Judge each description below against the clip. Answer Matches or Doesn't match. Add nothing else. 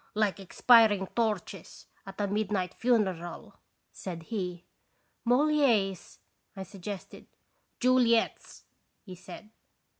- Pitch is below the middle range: Doesn't match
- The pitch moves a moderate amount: Matches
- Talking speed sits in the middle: Doesn't match